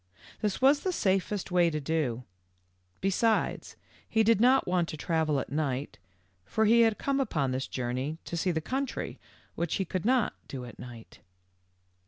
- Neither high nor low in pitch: Yes, medium, 175 Hz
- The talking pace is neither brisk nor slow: Yes, average, 170 wpm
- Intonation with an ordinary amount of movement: No, wide, 7.6 semitones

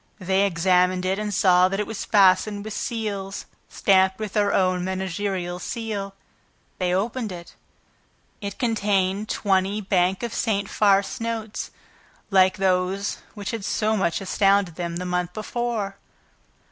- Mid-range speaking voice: No, high, 195 Hz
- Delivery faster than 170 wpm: No, average, 140 wpm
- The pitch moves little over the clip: Yes, narrow, 2.1 semitones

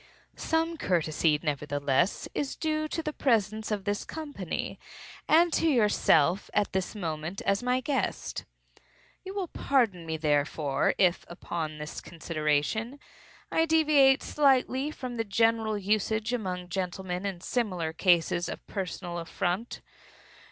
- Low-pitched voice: No, high, 200 Hz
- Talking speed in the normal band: No, slow, 130 wpm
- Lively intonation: Yes, wide, 7.1 semitones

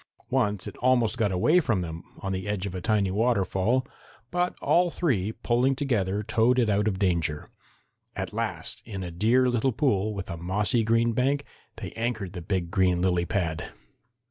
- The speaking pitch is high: No, low, 105 Hz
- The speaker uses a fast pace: No, average, 180 wpm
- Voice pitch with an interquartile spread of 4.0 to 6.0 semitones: Yes, average, 4.6 semitones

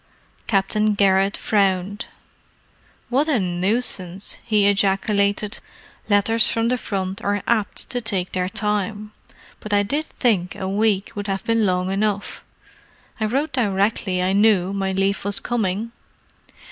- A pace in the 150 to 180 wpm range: No, slow, 135 wpm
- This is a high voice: Yes, high, 205 Hz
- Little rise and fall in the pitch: Yes, narrow, 2.1 semitones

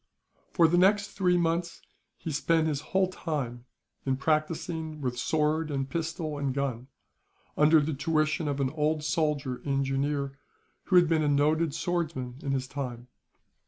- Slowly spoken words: No, average, 155 wpm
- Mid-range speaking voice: Yes, medium, 150 Hz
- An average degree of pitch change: Yes, average, 3.0 semitones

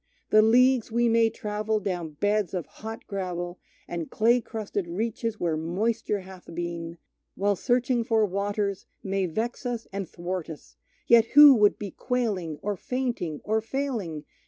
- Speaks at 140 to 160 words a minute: Yes, average, 155 wpm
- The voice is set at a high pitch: Yes, high, 210 Hz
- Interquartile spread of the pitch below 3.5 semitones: No, average, 4.3 semitones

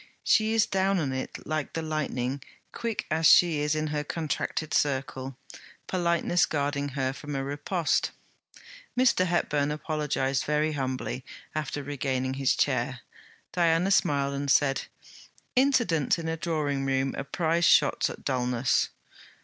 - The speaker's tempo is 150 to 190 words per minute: No, average, 140 wpm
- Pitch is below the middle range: No, medium, 150 Hz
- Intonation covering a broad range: No, average, 3.4 semitones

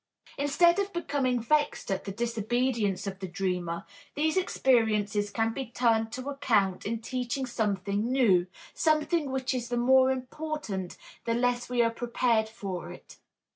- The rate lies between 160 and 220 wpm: No, average, 150 wpm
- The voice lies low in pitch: No, high, 240 Hz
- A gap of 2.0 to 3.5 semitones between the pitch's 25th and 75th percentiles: No, average, 4.1 semitones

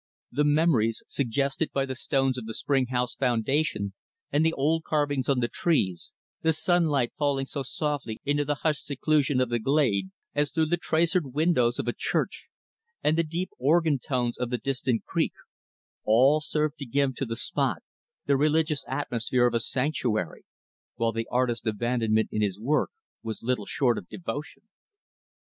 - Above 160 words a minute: Yes, average, 170 wpm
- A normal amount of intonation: Yes, average, 4.1 semitones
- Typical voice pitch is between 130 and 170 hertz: Yes, low, 135 Hz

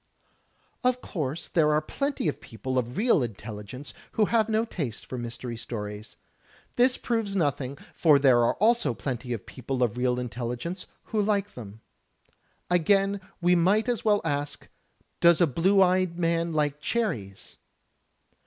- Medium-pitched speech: Yes, medium, 155 Hz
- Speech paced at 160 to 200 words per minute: No, average, 150 wpm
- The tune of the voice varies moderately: No, wide, 8.3 semitones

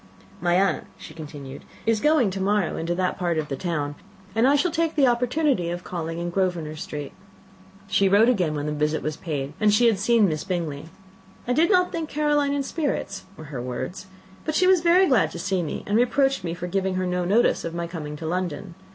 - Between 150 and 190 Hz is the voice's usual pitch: Yes, medium, 185 Hz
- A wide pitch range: Yes, wide, 7.4 semitones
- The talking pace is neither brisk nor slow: No, fast, 220 wpm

